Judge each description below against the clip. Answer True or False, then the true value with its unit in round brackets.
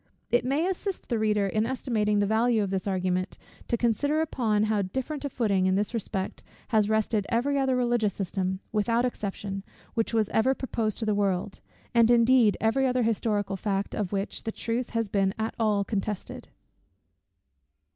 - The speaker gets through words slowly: False (175 wpm)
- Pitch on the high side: True (220 Hz)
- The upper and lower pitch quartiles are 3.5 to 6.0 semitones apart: False (3.1 semitones)